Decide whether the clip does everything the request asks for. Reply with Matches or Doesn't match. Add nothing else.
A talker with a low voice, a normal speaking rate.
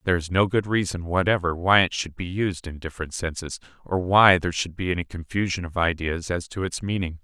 Doesn't match